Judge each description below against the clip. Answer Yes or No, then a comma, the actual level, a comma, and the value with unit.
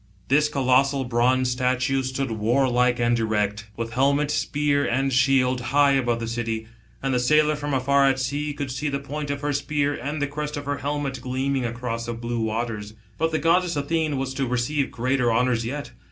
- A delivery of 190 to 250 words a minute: Yes, average, 195 wpm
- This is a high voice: No, low, 135 Hz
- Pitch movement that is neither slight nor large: Yes, average, 3.0 semitones